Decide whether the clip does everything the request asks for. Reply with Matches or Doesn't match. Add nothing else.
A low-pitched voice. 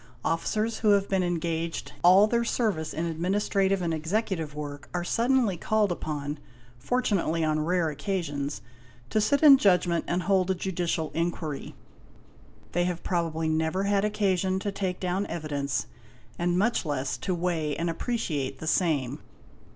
Doesn't match